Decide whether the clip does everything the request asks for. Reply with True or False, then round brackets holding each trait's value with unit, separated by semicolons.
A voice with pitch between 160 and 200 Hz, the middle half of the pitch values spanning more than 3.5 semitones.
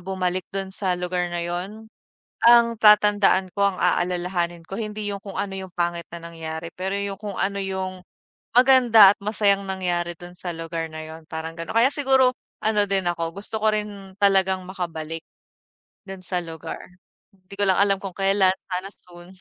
False (190 Hz; 2.5 semitones)